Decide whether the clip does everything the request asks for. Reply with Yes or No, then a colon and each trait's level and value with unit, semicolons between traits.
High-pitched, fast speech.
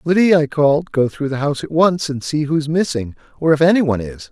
No: medium, 150 Hz; fast, 265 wpm